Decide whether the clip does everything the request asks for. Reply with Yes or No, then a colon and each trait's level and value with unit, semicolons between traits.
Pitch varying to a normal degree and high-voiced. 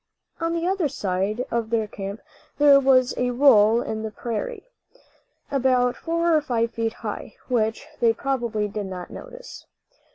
Yes: average, 4.4 semitones; high, 240 Hz